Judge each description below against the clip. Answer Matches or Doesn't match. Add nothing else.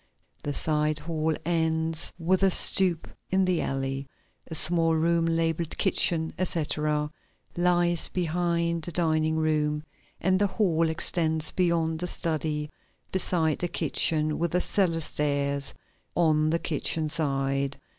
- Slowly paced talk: Matches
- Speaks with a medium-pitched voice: Matches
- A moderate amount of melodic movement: Doesn't match